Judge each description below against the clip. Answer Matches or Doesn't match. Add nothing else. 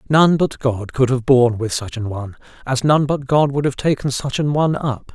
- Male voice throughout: Matches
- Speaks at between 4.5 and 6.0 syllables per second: Matches